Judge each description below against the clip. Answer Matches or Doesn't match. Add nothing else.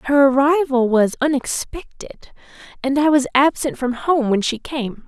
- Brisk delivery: Doesn't match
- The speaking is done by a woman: Matches